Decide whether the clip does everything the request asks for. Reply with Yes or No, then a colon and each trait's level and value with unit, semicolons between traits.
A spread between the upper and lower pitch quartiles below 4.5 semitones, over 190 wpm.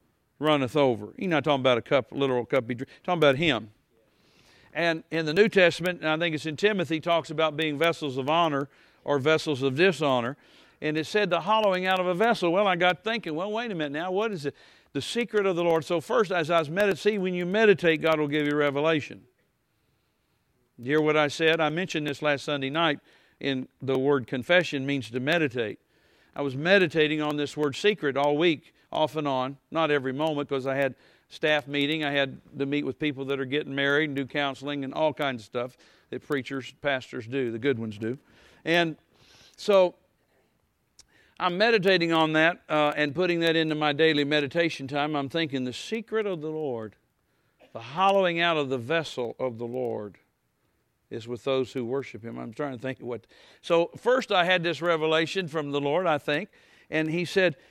Yes: average, 3.7 semitones; fast, 205 wpm